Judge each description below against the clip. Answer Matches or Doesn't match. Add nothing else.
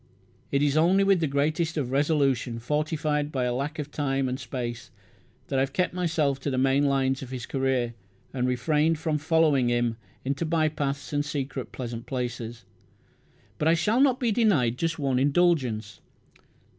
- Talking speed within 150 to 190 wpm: Matches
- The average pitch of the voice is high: Doesn't match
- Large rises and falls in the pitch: Doesn't match